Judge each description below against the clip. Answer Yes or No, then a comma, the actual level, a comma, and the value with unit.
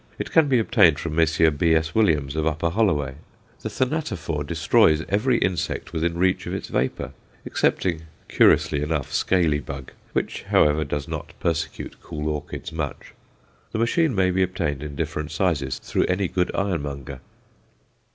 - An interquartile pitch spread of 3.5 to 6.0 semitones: Yes, average, 3.9 semitones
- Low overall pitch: Yes, very low, 80 Hz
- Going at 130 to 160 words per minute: Yes, average, 150 wpm